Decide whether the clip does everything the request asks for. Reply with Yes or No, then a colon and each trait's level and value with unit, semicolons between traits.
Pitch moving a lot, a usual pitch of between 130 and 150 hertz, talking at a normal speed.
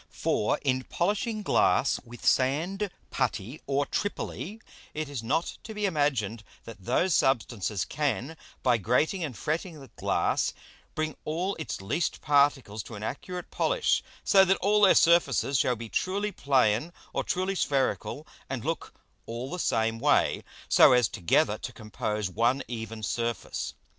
Yes: wide, 7.0 semitones; medium, 140 Hz; average, 150 wpm